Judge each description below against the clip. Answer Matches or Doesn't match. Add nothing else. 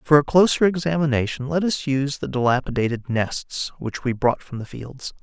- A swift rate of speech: Doesn't match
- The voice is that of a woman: Doesn't match